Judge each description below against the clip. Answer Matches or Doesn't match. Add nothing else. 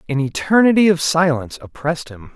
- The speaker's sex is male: Matches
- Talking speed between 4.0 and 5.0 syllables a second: Doesn't match